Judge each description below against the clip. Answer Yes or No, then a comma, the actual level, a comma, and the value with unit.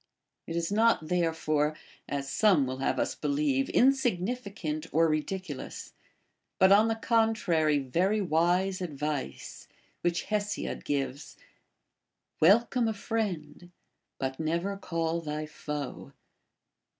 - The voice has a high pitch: No, medium, 165 Hz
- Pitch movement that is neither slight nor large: Yes, average, 5.0 semitones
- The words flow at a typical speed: No, slow, 115 wpm